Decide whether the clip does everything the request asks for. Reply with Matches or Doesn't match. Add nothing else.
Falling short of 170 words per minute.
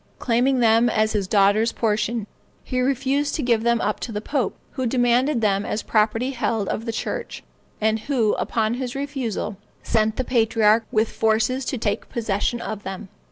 Doesn't match